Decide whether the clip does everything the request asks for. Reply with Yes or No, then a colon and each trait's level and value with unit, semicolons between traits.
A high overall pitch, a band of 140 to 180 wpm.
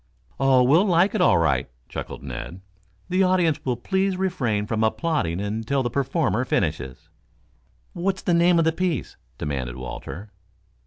No: low, 135 Hz; average, 150 wpm